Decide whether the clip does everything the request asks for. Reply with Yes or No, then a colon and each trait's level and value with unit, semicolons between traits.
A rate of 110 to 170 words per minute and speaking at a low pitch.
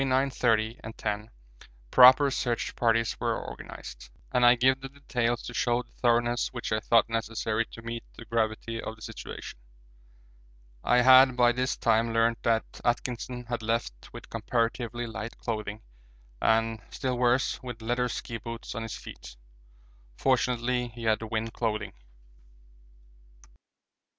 Yes: average, 140 wpm; low, 115 Hz